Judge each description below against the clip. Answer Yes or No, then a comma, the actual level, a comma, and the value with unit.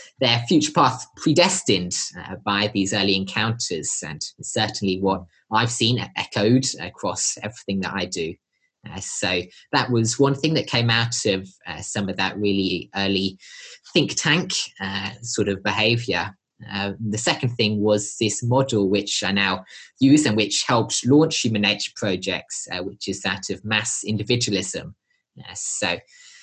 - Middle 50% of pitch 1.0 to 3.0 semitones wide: No, average, 3.7 semitones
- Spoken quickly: No, average, 155 wpm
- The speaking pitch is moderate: No, low, 105 Hz